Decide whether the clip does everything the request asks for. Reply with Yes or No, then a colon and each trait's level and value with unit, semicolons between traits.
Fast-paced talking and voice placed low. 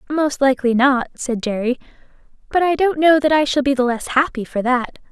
No: fast, 210 wpm; very high, 270 Hz